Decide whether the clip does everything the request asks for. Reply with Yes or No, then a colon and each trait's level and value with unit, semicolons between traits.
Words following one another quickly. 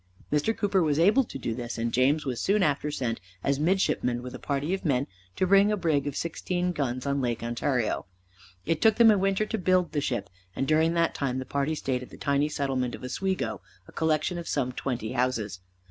Yes: fast, 220 wpm